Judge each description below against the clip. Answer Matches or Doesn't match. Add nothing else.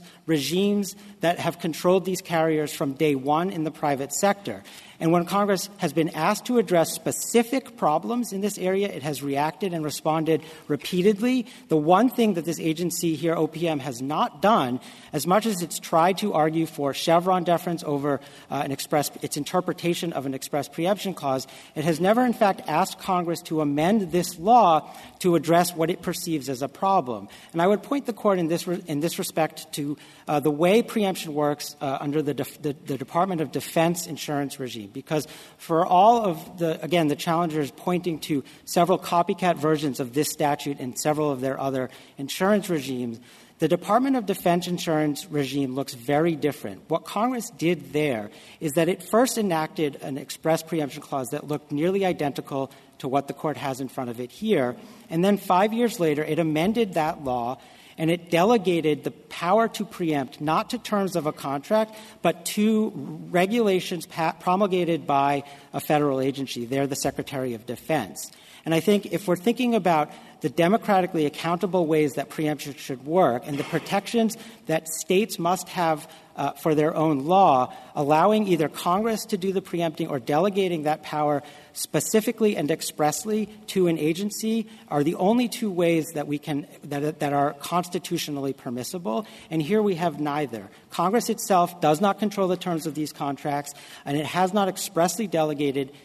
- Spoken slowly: Doesn't match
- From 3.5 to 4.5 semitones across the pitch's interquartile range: Matches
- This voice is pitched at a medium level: Matches